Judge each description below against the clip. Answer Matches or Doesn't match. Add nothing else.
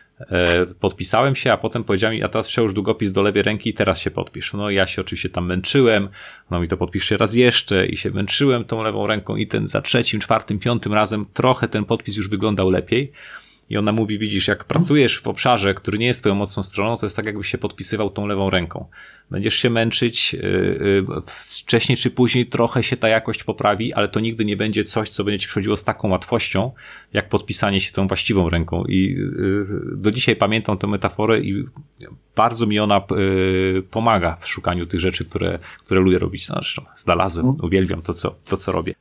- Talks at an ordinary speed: Doesn't match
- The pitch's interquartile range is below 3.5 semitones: Matches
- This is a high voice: Doesn't match